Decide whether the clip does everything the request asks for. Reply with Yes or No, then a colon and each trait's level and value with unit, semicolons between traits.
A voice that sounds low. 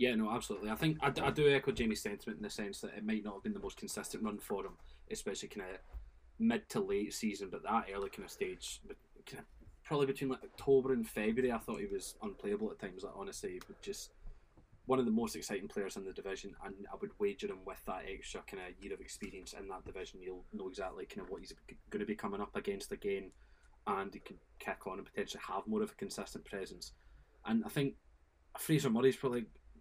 No: medium, 145 Hz